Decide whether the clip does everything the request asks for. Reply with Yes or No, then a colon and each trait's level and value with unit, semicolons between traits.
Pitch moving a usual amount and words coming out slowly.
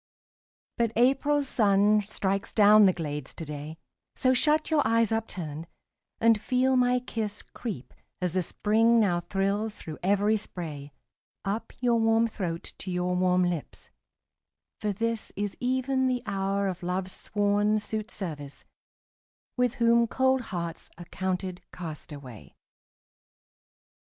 Yes: average, 4.3 semitones; slow, 130 wpm